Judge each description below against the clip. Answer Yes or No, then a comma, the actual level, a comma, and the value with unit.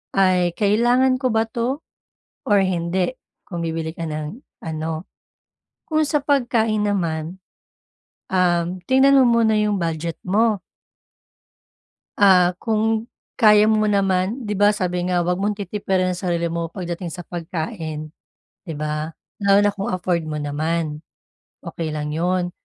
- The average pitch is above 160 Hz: Yes, medium, 185 Hz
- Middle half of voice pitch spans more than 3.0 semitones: Yes, average, 4.1 semitones